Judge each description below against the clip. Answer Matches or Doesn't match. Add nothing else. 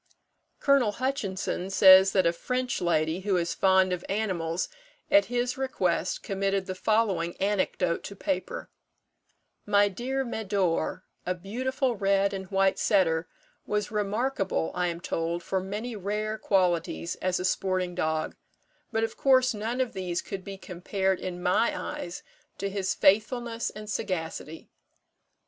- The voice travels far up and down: Doesn't match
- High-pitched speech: Matches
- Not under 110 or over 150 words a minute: Matches